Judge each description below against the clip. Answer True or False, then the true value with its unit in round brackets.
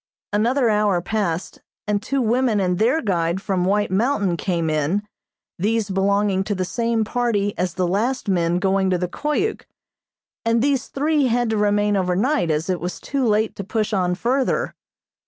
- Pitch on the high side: True (205 Hz)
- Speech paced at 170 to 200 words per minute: True (175 wpm)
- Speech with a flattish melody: False (4.1 semitones)